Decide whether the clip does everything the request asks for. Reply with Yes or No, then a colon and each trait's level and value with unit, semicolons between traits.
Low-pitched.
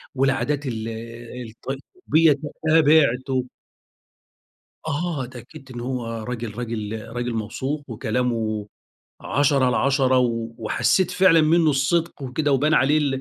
Yes: low, 130 Hz